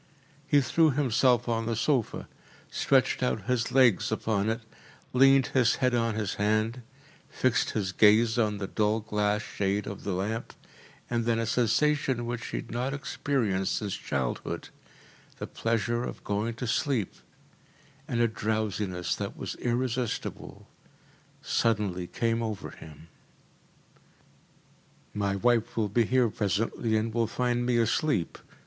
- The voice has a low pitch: Yes, low, 115 Hz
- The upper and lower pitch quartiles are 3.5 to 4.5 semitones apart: No, average, 2.8 semitones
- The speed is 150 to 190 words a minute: No, average, 140 wpm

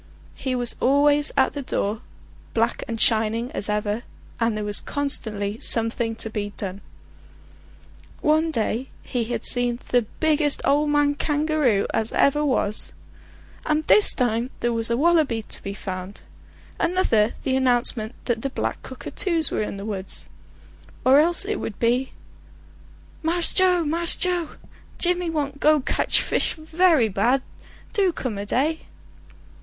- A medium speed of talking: Yes, average, 150 wpm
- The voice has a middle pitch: No, very high, 255 Hz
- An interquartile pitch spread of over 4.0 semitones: Yes, wide, 5.6 semitones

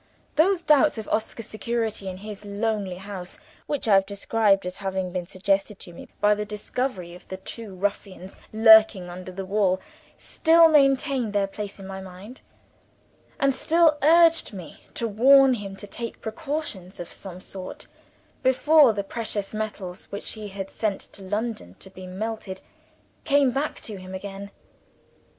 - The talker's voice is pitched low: No, high, 205 Hz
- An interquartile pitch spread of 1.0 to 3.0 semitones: No, average, 3.9 semitones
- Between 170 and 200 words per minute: No, average, 160 wpm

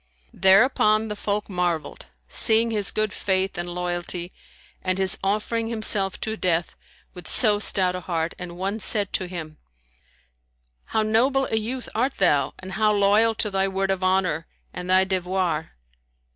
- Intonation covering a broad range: No, average, 3.2 semitones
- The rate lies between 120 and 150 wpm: No, average, 160 wpm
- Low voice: No, high, 195 Hz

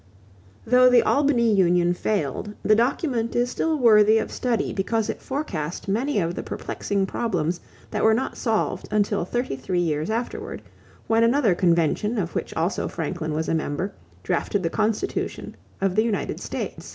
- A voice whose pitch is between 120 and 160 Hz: No, high, 210 Hz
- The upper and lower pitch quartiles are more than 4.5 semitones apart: Yes, average, 5.0 semitones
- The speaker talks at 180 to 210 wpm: No, average, 165 wpm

